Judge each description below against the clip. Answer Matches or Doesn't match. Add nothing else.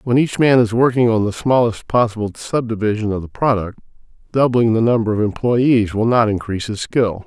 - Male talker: Matches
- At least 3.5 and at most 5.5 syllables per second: Matches